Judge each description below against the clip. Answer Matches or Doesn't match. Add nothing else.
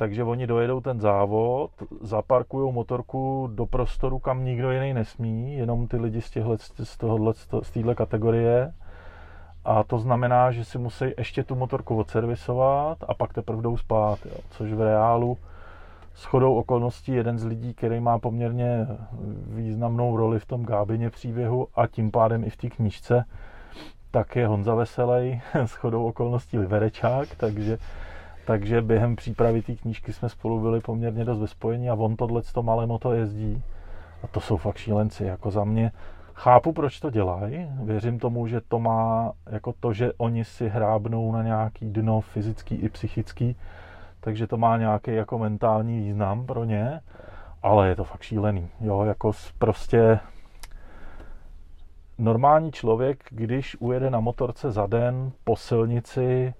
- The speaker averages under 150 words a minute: Doesn't match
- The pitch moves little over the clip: Matches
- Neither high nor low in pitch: Doesn't match